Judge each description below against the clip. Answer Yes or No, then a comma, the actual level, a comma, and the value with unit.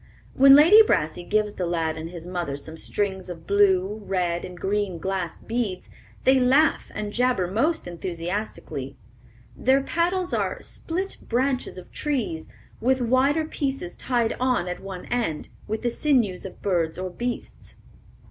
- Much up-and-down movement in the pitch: Yes, wide, 6.5 semitones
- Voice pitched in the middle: No, high, 205 Hz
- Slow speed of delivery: No, average, 150 wpm